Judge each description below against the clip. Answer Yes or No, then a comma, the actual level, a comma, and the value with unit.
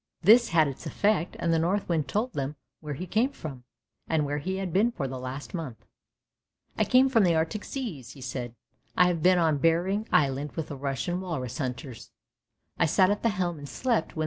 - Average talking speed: No, fast, 220 wpm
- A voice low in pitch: No, medium, 165 Hz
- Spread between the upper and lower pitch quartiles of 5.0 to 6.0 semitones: Yes, average, 5.3 semitones